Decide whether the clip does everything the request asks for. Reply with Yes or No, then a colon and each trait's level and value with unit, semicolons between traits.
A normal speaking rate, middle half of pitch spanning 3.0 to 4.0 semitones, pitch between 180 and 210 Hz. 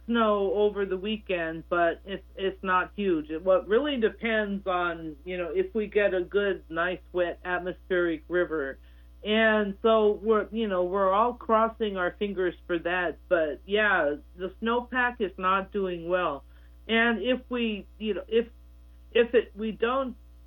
Yes: average, 165 wpm; average, 3.7 semitones; high, 190 Hz